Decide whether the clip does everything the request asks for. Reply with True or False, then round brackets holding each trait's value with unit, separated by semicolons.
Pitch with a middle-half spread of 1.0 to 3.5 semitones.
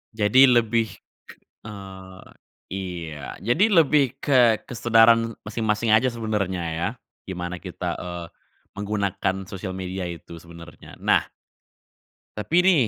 False (4.1 semitones)